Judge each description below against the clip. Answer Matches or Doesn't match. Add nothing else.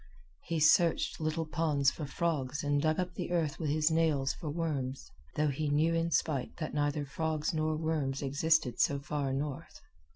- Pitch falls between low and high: Matches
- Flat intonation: Matches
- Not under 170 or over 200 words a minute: Matches